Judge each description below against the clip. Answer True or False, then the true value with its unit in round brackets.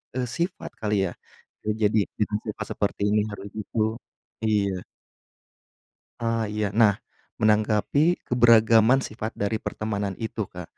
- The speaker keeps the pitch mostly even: True (1.8 semitones)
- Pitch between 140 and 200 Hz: False (110 Hz)